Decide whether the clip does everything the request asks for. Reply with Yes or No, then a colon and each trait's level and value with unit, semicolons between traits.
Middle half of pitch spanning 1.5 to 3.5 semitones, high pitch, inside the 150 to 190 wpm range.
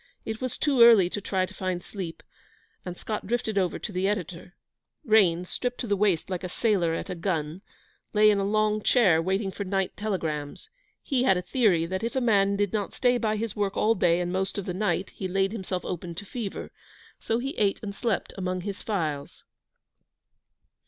No: average, 3.1 semitones; high, 195 Hz; fast, 205 wpm